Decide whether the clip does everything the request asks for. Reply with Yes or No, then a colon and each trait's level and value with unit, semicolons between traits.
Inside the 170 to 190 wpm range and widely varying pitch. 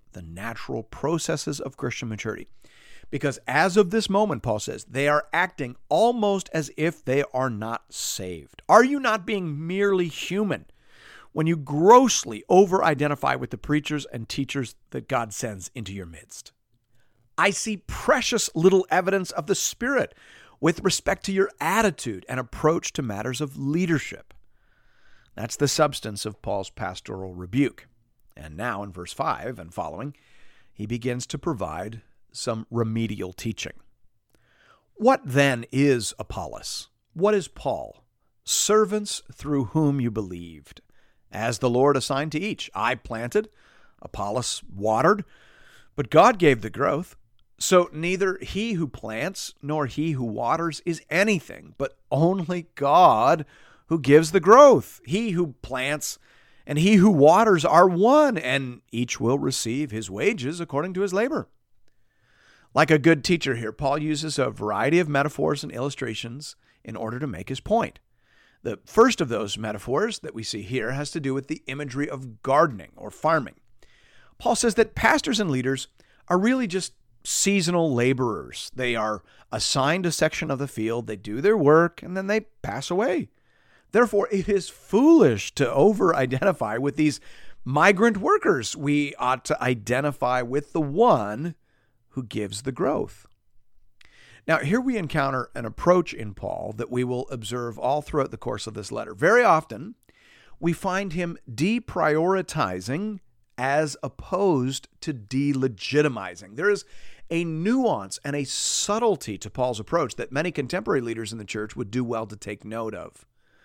No: average, 155 wpm; wide, 7.1 semitones